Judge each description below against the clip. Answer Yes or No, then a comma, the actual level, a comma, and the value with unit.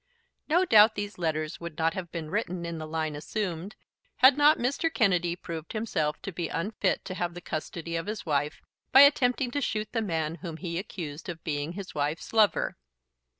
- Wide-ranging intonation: No, average, 5.0 semitones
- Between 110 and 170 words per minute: No, average, 195 wpm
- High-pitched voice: No, medium, 175 Hz